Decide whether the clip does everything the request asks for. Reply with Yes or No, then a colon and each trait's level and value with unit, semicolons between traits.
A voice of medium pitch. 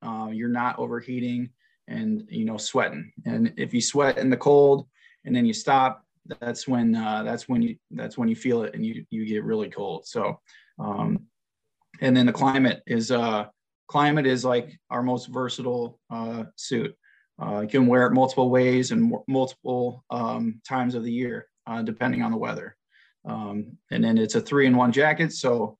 No: low, 130 Hz